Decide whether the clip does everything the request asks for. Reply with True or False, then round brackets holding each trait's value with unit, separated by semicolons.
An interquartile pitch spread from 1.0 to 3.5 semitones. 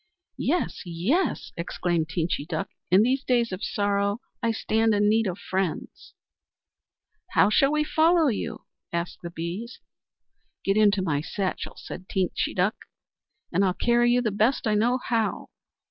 False (4.5 semitones)